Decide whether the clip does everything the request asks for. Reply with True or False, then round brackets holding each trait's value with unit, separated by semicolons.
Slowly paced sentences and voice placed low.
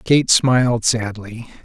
True (110 wpm; 120 Hz)